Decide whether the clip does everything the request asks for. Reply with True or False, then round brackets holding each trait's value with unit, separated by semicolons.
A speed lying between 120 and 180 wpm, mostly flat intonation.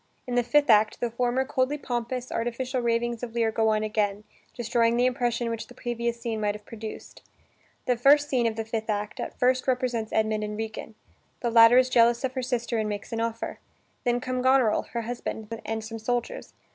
False (205 wpm; 2.0 semitones)